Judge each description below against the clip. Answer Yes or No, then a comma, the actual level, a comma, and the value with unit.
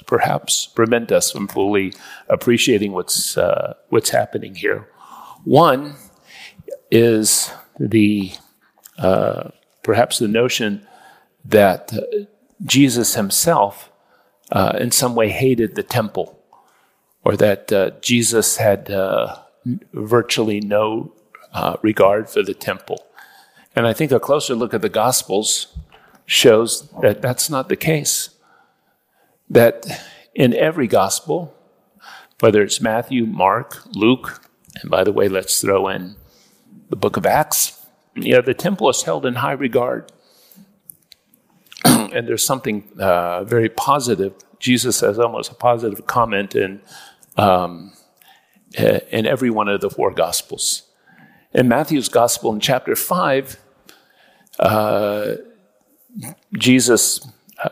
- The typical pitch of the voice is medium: No, low, 115 Hz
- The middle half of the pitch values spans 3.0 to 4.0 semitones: No, average, 4.5 semitones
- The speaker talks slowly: Yes, slow, 120 wpm